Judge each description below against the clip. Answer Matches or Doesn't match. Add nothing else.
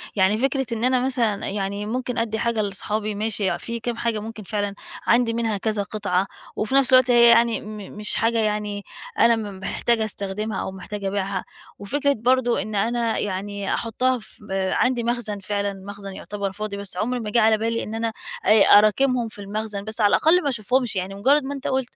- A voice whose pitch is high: Matches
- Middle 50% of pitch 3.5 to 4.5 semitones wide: Doesn't match